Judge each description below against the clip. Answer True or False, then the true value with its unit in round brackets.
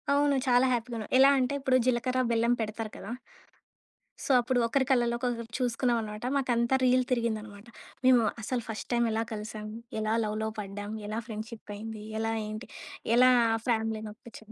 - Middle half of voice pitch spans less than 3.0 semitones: True (2.6 semitones)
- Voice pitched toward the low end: False (230 Hz)